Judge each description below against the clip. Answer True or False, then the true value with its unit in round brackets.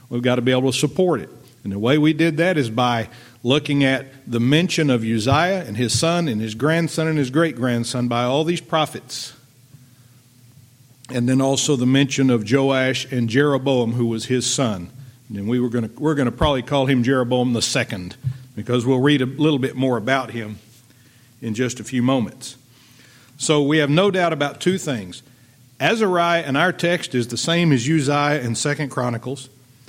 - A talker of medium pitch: False (130 Hz)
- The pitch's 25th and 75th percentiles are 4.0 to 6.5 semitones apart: False (2.9 semitones)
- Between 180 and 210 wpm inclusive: True (195 wpm)